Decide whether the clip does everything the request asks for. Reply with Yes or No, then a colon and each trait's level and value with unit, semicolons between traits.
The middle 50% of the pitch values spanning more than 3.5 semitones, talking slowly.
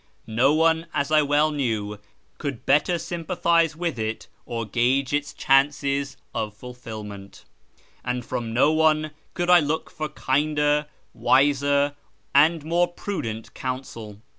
Yes: average, 4.1 semitones; slow, 130 wpm